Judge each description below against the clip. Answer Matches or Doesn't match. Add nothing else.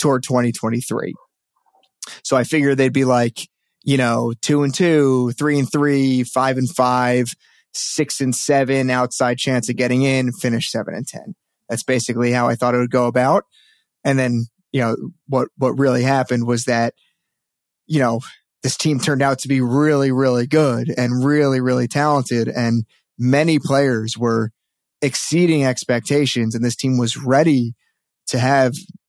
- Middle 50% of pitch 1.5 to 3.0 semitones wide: Matches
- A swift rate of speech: Doesn't match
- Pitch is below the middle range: Matches